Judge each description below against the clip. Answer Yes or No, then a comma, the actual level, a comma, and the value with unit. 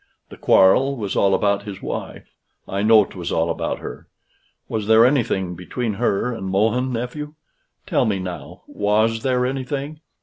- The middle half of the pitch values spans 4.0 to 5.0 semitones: Yes, average, 4.3 semitones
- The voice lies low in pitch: Yes, low, 110 Hz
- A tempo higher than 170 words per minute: No, average, 160 wpm